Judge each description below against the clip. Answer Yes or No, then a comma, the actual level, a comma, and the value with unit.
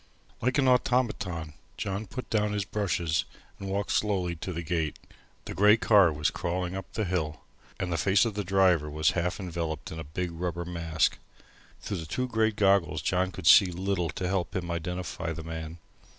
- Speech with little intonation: No, average, 3.3 semitones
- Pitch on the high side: No, very low, 90 Hz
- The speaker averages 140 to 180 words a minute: No, average, 190 wpm